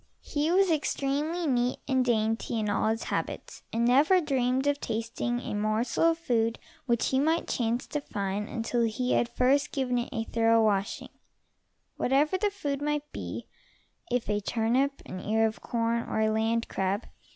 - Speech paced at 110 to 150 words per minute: No, average, 175 wpm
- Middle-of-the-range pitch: No, high, 240 Hz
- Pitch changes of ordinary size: Yes, average, 4.0 semitones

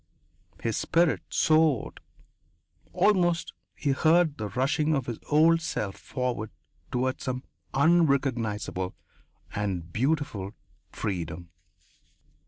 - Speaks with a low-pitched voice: Yes, low, 130 Hz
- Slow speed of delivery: Yes, slow, 90 wpm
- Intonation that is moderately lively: No, wide, 7.0 semitones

